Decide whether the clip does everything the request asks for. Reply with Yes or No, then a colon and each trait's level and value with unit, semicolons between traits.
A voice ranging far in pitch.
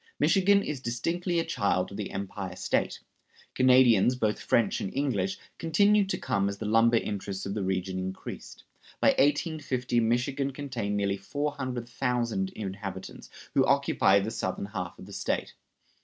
Yes: wide, 5.7 semitones